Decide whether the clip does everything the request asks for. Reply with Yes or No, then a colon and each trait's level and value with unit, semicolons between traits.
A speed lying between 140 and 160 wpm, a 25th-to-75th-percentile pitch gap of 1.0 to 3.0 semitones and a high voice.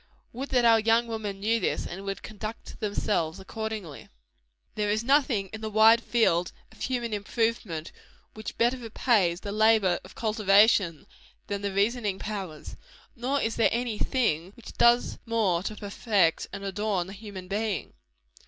Yes: average, 155 wpm; average, 2.7 semitones; high, 215 Hz